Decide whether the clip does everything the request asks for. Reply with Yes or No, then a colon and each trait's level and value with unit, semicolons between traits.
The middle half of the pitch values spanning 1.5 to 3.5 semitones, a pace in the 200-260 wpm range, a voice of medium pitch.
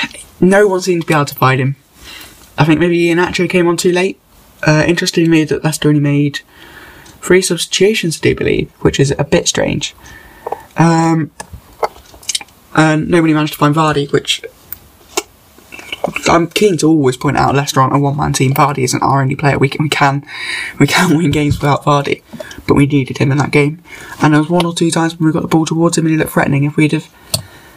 Yes: average, 2.9 semitones; fast, 205 wpm; medium, 155 Hz